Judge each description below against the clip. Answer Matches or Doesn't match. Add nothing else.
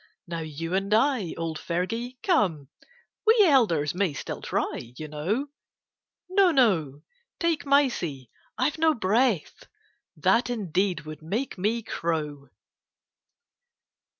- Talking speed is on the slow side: Matches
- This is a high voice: Matches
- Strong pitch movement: Matches